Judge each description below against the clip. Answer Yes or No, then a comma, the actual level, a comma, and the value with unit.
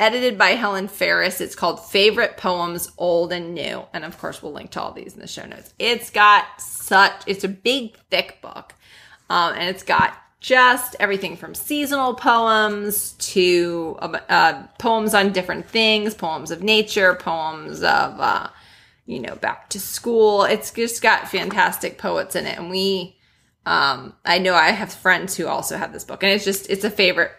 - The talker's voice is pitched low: No, high, 200 Hz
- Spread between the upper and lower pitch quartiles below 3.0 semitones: No, average, 3.6 semitones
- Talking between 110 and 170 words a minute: No, average, 180 wpm